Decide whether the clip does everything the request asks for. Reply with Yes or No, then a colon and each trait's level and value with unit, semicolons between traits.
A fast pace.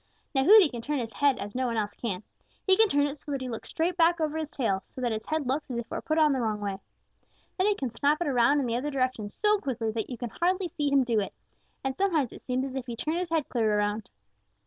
Yes: fast, 285 wpm